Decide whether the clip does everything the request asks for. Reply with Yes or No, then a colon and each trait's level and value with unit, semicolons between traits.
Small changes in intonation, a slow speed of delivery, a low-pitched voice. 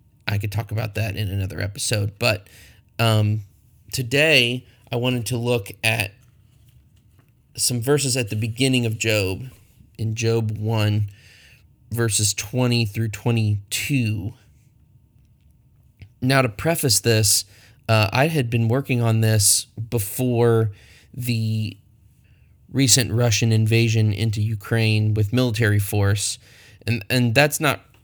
Yes: narrow, 2.3 semitones; slow, 120 wpm; low, 115 Hz